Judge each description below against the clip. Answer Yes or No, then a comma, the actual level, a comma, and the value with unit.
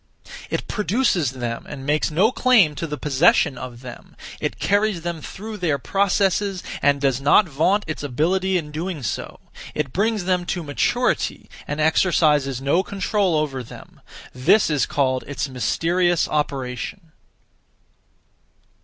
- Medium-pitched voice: Yes, medium, 155 Hz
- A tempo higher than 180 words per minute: No, average, 140 wpm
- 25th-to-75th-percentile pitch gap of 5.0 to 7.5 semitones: Yes, wide, 5.4 semitones